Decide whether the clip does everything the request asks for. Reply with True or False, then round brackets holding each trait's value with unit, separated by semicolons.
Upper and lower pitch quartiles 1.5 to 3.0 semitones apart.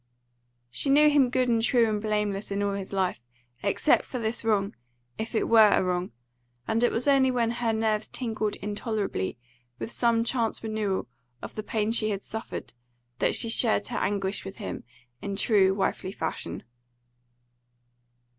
True (2.5 semitones)